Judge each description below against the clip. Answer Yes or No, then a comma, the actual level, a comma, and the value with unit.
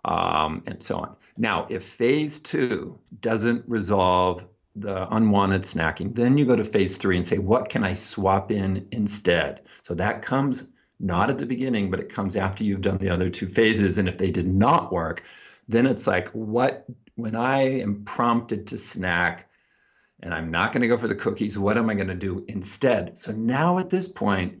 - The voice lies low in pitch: Yes, low, 105 Hz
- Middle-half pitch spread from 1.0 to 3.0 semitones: No, average, 3.8 semitones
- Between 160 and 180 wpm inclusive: No, average, 200 wpm